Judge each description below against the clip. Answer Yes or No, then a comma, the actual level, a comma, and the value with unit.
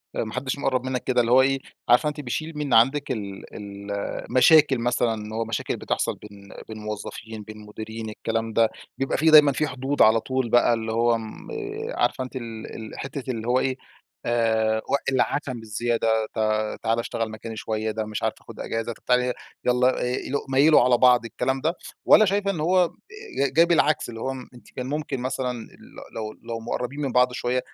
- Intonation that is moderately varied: Yes, average, 3.1 semitones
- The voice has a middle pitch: No, low, 120 Hz